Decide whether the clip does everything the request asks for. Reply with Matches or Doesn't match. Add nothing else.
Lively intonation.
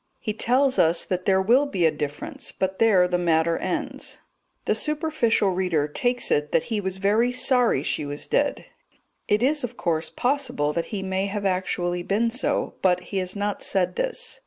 Matches